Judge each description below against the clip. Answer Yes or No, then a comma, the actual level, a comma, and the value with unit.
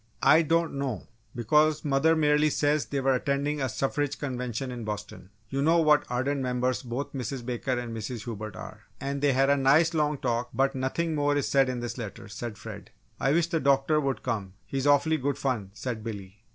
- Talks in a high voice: No, low, 135 Hz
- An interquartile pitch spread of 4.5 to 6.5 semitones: No, average, 3.1 semitones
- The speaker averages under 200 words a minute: No, fast, 205 wpm